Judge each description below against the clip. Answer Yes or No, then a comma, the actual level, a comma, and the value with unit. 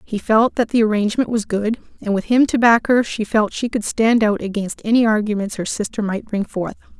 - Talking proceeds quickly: Yes, fast, 230 wpm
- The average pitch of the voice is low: No, high, 215 Hz